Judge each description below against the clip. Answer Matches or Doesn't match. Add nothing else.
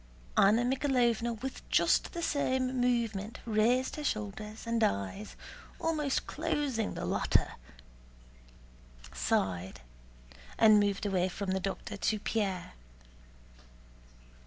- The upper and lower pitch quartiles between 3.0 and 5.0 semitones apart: Matches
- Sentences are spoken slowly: Matches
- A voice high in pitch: Matches